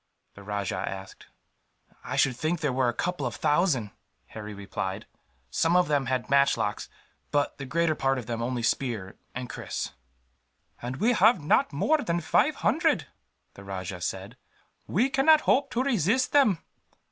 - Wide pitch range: Yes, wide, 8.5 semitones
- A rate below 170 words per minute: Yes, average, 160 wpm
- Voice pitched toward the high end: No, low, 135 Hz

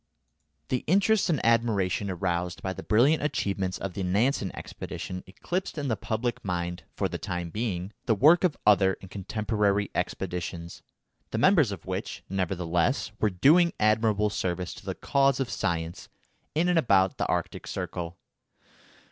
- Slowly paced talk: No, average, 155 wpm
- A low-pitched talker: Yes, low, 100 Hz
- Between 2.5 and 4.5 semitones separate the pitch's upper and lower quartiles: No, average, 5.2 semitones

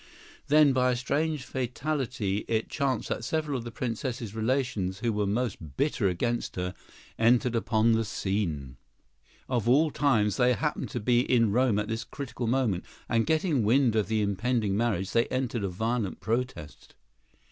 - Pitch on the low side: Yes, low, 115 Hz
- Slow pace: No, average, 165 wpm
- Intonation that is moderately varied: Yes, average, 3.5 semitones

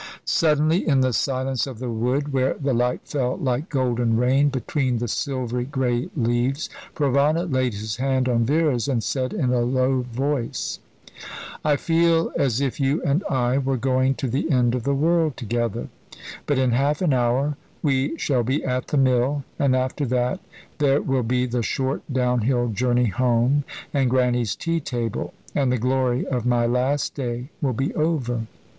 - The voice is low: Yes, low, 130 Hz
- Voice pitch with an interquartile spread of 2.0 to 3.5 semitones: Yes, narrow, 2.4 semitones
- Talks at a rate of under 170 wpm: No, average, 175 wpm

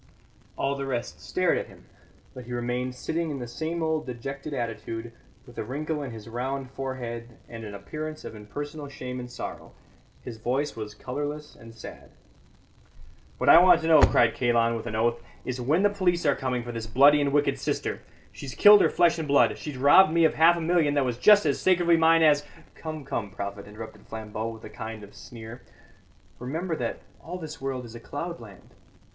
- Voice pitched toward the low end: Yes, low, 130 Hz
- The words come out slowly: No, average, 200 wpm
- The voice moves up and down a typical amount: Yes, average, 4.9 semitones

